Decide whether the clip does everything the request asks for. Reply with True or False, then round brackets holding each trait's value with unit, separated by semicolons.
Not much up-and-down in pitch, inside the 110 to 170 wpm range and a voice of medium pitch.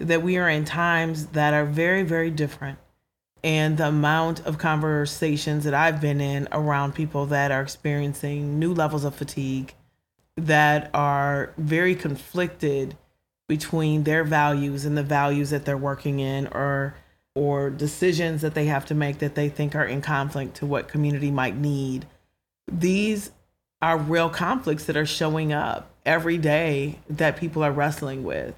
True (2.0 semitones; 160 wpm; 150 Hz)